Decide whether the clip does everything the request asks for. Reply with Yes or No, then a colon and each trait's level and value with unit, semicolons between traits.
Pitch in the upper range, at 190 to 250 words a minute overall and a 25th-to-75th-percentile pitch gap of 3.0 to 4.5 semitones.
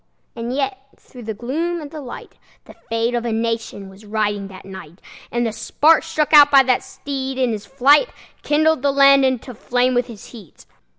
Yes: very high, 250 Hz; average, 195 wpm; average, 3.9 semitones